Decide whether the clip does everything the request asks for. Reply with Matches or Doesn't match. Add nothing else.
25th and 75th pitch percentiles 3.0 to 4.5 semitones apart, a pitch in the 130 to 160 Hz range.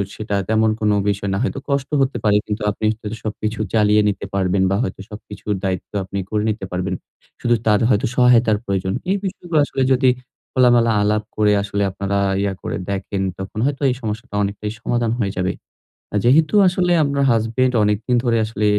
Doesn't match